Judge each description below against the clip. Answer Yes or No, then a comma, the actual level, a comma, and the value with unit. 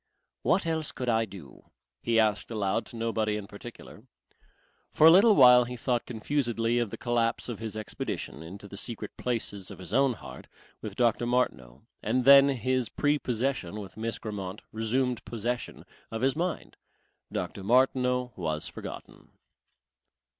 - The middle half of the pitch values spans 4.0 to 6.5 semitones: No, average, 3.2 semitones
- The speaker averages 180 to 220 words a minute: No, average, 155 wpm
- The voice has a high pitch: No, low, 115 Hz